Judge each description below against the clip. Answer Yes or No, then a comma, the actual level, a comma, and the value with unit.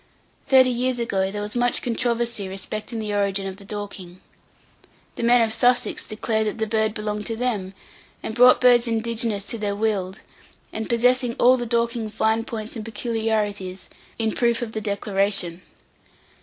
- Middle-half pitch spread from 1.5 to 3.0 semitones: Yes, narrow, 2.5 semitones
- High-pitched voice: Yes, high, 220 Hz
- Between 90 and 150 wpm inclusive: No, average, 165 wpm